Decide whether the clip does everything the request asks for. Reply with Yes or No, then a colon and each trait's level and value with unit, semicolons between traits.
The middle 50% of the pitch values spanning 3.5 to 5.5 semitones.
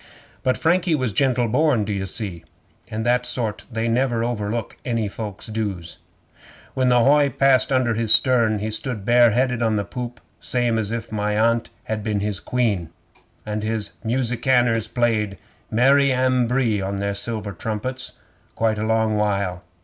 No: average, 2.8 semitones